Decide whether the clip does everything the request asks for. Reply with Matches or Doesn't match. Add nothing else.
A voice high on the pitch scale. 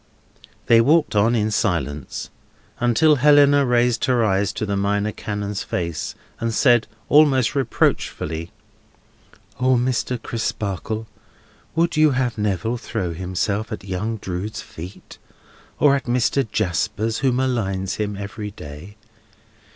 Doesn't match